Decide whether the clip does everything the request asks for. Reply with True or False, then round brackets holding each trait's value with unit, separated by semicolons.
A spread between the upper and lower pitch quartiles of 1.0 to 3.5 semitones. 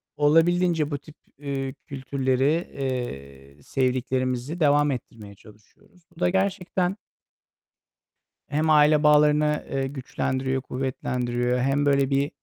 True (2.9 semitones)